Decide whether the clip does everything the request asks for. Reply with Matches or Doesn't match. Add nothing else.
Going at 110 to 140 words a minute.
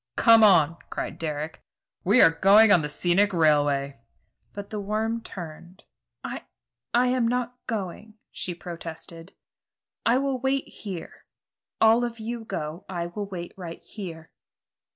Matches